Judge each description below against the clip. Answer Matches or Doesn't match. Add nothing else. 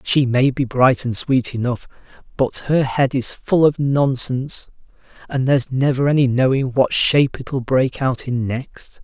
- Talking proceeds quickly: Doesn't match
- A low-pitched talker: Matches